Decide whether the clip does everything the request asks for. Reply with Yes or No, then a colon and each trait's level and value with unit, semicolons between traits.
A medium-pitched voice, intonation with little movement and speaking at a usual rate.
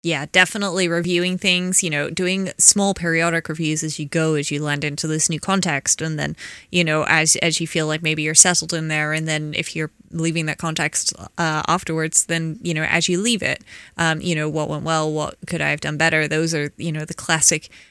No: medium, 160 Hz; narrow, 1.8 semitones; fast, 230 wpm